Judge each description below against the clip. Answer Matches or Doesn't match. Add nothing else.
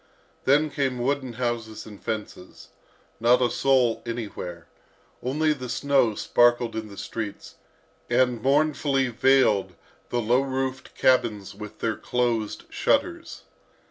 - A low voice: Matches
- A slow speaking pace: Matches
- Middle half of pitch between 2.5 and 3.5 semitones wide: Matches